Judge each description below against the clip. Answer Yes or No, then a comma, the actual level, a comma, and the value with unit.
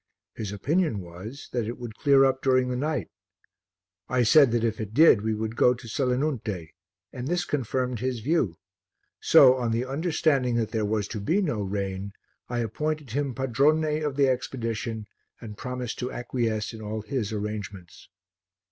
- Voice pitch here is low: Yes, low, 120 Hz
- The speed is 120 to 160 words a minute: No, average, 170 wpm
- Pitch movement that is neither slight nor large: Yes, average, 3.9 semitones